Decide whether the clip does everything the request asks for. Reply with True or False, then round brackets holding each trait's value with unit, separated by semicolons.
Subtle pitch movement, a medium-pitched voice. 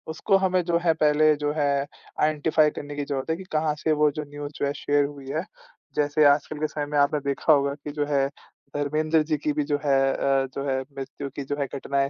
True (1.5 semitones; 145 Hz)